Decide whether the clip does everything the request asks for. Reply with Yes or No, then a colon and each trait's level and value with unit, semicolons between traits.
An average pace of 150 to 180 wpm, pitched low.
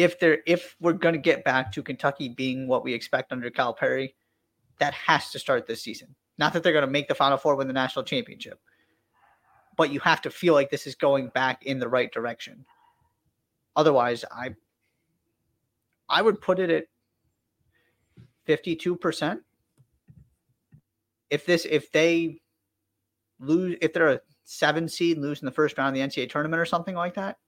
No: average, 175 wpm; medium, 145 Hz